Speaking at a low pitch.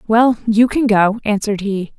No: high, 215 Hz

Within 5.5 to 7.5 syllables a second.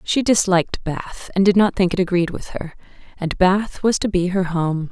No: 4.8 syllables/s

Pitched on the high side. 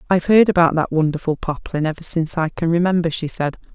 No: medium, 165 Hz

